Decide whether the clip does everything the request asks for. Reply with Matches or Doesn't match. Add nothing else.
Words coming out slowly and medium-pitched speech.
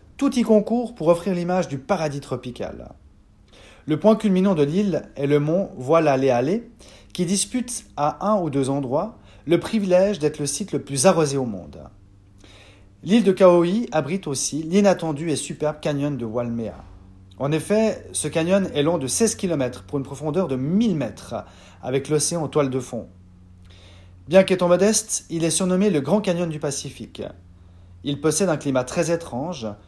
Doesn't match